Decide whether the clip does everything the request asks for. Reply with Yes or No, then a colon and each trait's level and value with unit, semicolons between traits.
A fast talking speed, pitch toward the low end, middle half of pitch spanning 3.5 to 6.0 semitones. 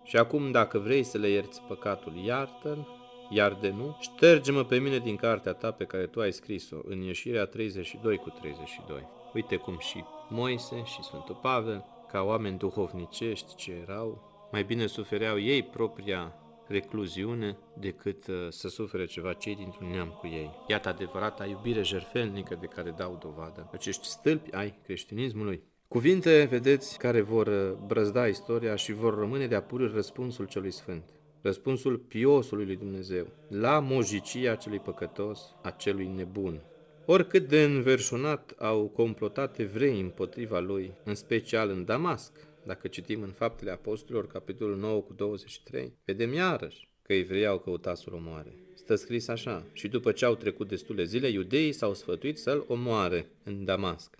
No: average, 150 wpm; low, 105 Hz; average, 4.5 semitones